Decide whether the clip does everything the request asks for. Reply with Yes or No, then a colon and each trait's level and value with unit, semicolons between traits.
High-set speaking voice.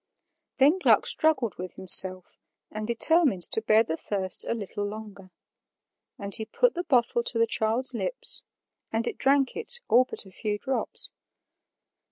Yes: high, 225 Hz